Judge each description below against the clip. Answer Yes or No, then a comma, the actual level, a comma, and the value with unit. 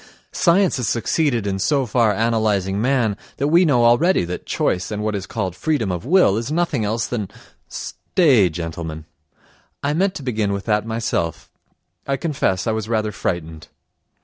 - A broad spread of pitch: Yes, wide, 6.0 semitones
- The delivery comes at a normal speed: Yes, average, 170 wpm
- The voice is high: No, low, 110 Hz